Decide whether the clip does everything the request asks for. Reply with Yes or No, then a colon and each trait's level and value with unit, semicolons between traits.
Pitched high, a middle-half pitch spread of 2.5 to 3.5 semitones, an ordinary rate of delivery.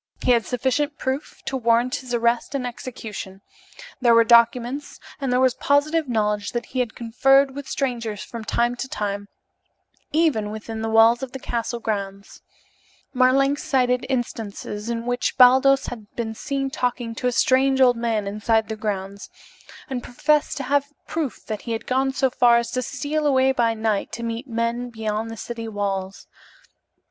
Yes: high, 240 Hz; average, 3.0 semitones; average, 175 wpm